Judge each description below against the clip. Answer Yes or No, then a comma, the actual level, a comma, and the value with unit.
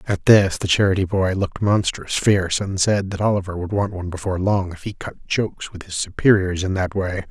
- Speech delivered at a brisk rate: Yes, fast, 220 wpm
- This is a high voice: No, very low, 95 Hz